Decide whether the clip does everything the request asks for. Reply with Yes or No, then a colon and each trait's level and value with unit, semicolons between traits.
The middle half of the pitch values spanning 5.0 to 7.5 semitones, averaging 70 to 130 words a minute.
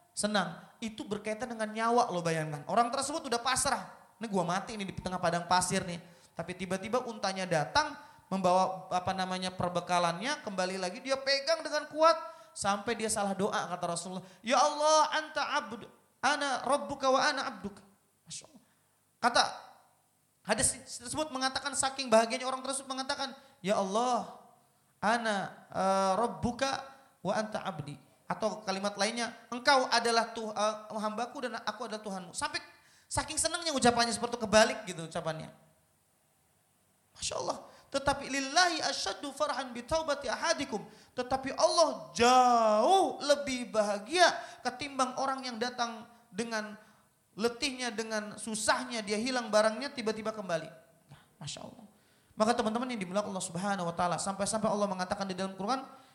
No: wide, 5.6 semitones; fast, 140 wpm